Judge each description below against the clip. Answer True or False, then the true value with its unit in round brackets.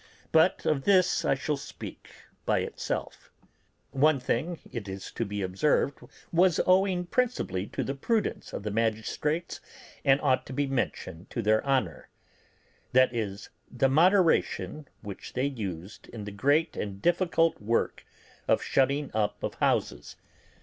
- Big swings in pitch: True (7.2 semitones)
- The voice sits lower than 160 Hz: True (135 Hz)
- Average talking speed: True (145 wpm)